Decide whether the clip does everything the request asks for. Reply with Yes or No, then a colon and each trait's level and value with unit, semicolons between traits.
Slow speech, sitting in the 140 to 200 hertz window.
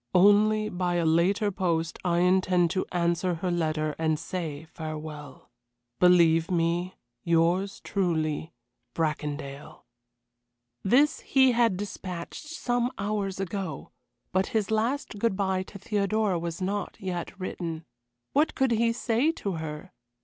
Yes: slow, 130 wpm; medium, 185 Hz